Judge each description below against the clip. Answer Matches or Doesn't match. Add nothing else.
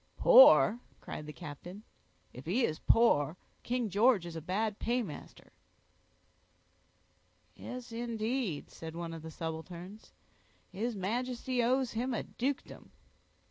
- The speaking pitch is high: Matches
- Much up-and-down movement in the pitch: Matches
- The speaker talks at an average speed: Doesn't match